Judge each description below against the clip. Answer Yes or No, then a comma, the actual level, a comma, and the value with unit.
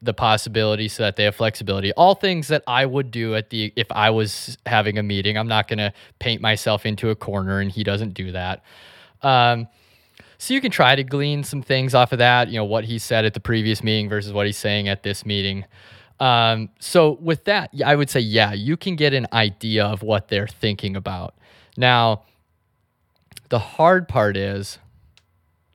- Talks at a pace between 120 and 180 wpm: No, average, 200 wpm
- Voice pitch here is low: Yes, low, 110 Hz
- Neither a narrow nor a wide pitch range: Yes, average, 3.2 semitones